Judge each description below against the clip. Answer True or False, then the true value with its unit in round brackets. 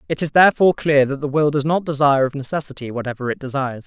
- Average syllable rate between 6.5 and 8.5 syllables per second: True (7.3 syllables/s)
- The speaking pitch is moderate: True (145 Hz)